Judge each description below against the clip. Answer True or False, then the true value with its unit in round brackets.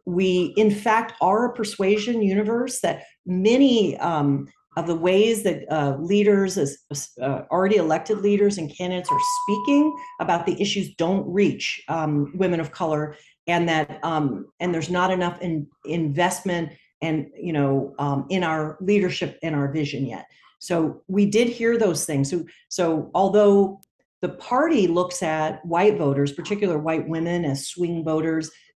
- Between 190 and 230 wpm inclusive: False (155 wpm)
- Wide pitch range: False (4.4 semitones)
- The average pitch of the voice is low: False (175 Hz)